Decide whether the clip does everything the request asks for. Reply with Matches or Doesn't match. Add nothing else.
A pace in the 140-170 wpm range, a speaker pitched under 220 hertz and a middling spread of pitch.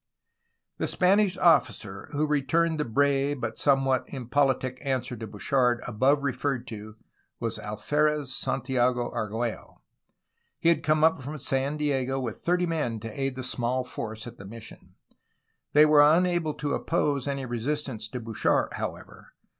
Matches